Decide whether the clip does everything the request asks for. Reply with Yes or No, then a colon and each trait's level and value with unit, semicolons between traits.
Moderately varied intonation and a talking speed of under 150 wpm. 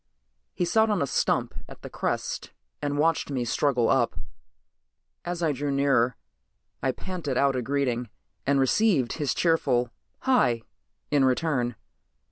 Yes: average, 4.5 semitones; average, 140 wpm